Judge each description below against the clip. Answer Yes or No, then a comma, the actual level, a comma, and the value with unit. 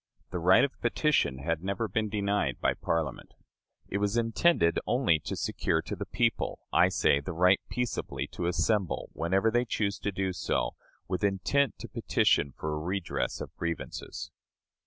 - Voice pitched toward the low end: Yes, very low, 95 Hz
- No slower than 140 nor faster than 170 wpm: Yes, average, 165 wpm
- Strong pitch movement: No, average, 4.4 semitones